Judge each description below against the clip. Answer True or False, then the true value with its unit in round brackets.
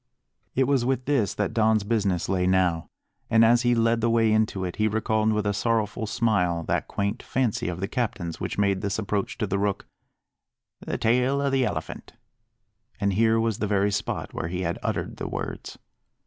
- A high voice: False (110 Hz)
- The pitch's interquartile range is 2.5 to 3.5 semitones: True (2.8 semitones)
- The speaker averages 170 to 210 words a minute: True (195 wpm)